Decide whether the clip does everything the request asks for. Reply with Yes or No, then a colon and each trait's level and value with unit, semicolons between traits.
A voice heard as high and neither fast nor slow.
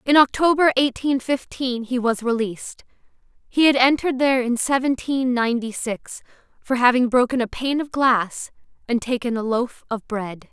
Yes: very high, 250 Hz; average, 160 wpm